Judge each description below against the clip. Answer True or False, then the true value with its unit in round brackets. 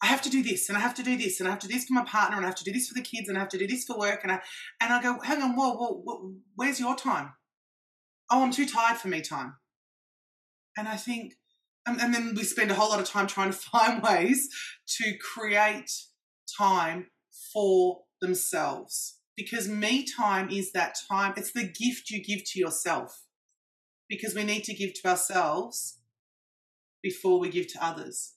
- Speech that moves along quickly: True (220 wpm)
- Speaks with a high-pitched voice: True (210 Hz)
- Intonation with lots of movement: False (4.1 semitones)